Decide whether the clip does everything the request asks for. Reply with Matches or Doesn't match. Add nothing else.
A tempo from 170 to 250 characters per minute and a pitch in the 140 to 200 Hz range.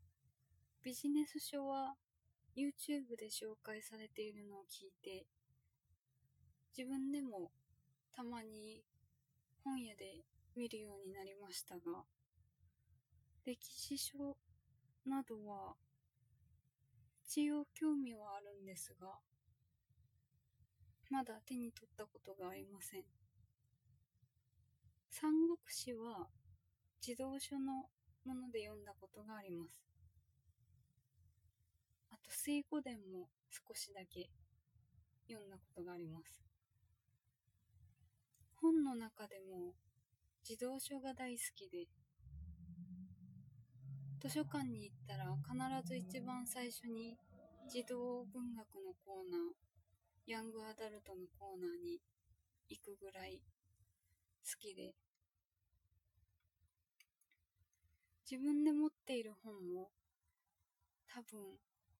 Matches